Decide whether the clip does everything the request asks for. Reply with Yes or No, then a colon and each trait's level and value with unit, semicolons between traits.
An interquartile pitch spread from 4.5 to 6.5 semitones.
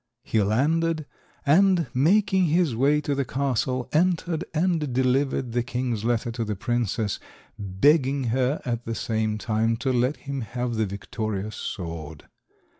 Yes: average, 4.8 semitones